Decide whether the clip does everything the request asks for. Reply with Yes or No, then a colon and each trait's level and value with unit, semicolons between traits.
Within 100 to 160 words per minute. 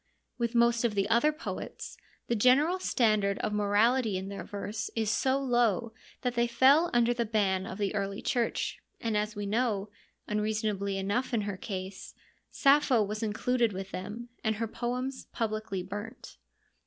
No: average, 170 wpm